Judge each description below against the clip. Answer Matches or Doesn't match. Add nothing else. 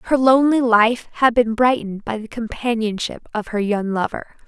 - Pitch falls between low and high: Doesn't match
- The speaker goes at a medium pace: Matches